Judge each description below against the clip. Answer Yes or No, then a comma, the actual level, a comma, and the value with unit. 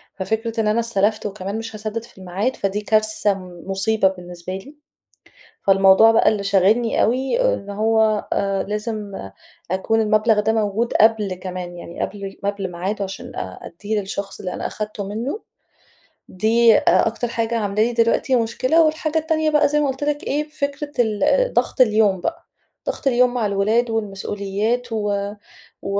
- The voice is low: No, high, 215 Hz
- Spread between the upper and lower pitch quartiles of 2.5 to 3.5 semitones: Yes, average, 3.0 semitones